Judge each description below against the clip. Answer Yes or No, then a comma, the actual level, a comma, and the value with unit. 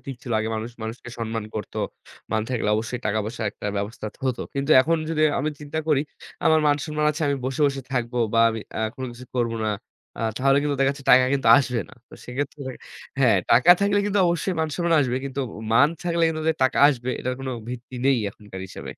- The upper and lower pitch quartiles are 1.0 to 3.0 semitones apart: No, average, 4.1 semitones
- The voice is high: No, low, 130 Hz